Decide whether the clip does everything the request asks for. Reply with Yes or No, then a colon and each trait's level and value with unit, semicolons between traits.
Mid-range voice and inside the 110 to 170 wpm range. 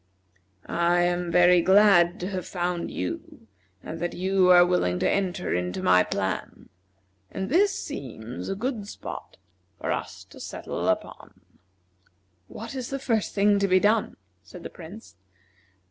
Yes: medium, 180 Hz; average, 150 wpm